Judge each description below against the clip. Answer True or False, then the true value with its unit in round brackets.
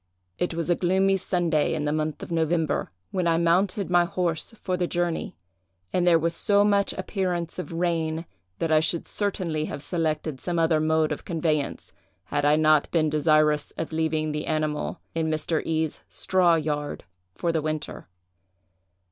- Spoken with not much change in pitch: True (2.1 semitones)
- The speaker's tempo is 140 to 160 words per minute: False (170 wpm)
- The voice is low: False (165 Hz)